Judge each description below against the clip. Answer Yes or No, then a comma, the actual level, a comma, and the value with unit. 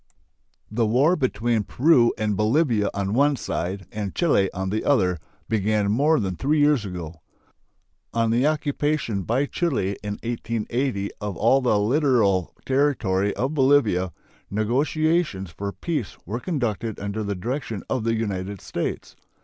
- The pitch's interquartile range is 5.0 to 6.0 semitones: Yes, wide, 5.5 semitones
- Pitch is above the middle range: No, low, 115 Hz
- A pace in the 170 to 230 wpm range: No, average, 145 wpm